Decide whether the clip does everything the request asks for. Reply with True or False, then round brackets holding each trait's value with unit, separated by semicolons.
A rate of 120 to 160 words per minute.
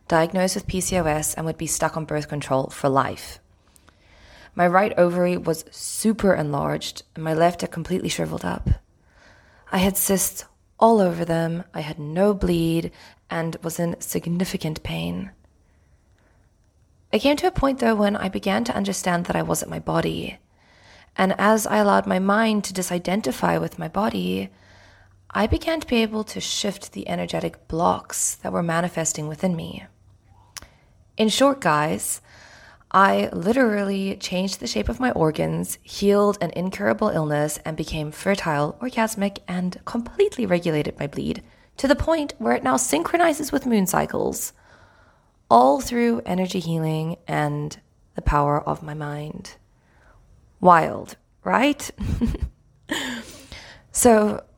True (140 wpm)